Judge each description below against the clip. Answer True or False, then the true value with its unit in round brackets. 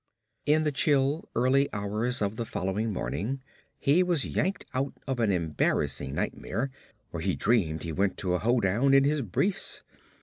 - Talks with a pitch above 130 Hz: False (115 Hz)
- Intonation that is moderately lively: False (6.4 semitones)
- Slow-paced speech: False (165 wpm)